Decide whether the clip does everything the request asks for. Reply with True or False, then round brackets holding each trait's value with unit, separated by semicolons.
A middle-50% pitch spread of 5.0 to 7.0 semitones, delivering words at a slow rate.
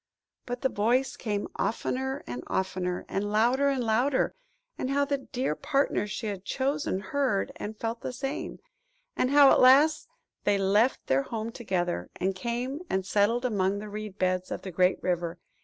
False (5.5 semitones; 175 wpm)